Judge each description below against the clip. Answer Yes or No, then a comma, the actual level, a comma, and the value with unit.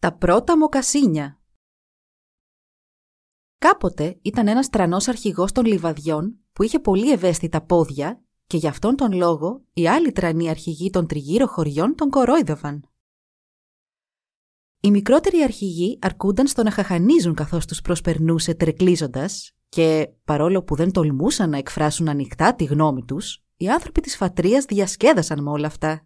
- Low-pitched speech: No, medium, 175 Hz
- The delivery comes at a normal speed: Yes, average, 135 wpm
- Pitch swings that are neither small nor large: No, wide, 5.8 semitones